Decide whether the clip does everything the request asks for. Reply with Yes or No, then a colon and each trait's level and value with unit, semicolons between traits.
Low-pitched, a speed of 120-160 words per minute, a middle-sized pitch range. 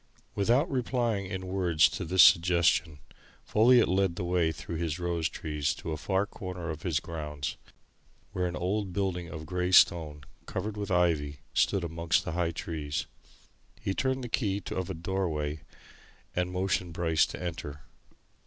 Yes: very low, 90 Hz; average, 155 wpm; average, 3.0 semitones